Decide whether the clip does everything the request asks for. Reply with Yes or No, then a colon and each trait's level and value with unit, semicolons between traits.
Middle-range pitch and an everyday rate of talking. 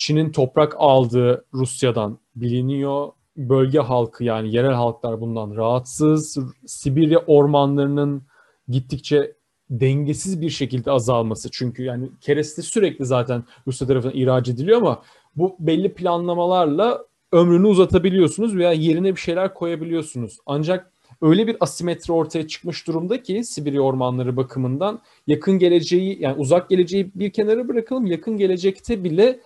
Yes: medium, 150 Hz; average, 125 wpm